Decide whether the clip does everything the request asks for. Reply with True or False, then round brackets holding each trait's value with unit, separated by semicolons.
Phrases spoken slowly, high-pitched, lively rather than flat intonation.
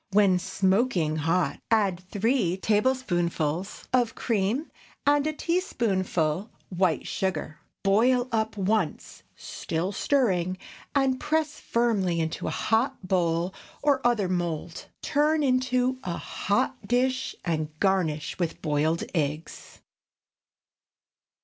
True (105 wpm; 195 Hz; 6.5 semitones)